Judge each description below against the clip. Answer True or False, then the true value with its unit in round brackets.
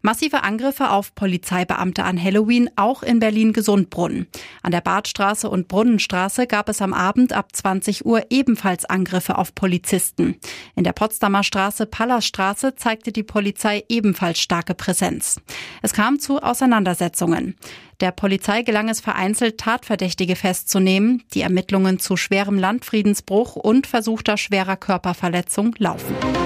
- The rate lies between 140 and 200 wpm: False (130 wpm)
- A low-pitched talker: False (200 Hz)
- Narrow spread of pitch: False (3.0 semitones)